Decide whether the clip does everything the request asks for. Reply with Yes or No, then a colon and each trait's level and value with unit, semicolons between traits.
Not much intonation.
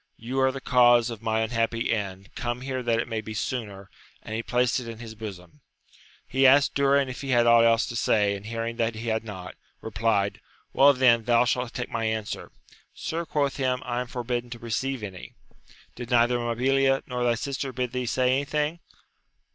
Yes: narrow, 2.3 semitones